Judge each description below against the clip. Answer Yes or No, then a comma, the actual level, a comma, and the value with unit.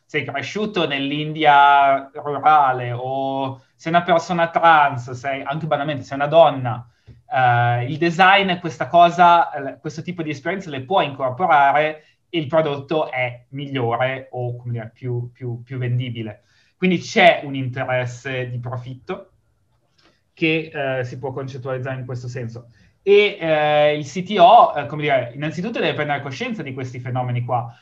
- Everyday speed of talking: Yes, average, 145 wpm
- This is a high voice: No, medium, 140 Hz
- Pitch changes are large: No, average, 4.2 semitones